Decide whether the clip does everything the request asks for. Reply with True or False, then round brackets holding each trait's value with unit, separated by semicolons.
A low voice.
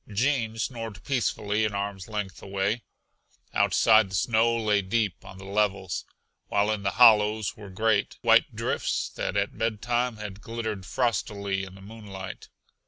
True (105 Hz)